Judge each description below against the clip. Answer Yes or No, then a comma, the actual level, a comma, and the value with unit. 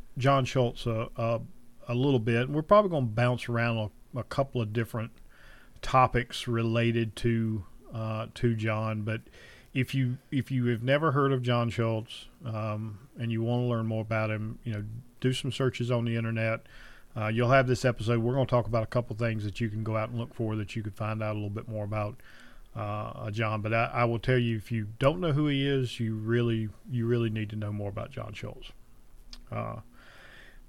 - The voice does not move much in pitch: Yes, narrow, 2.2 semitones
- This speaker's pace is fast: Yes, fast, 215 wpm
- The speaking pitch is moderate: No, low, 115 Hz